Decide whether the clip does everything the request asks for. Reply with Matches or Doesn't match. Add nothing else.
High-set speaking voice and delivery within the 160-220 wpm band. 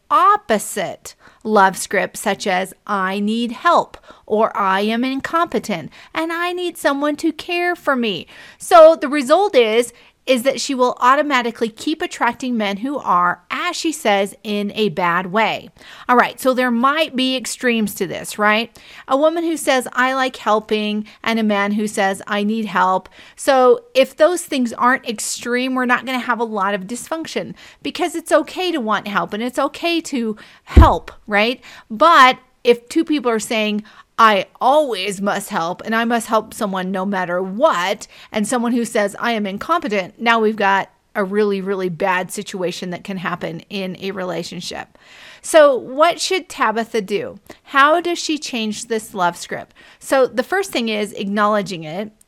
Matches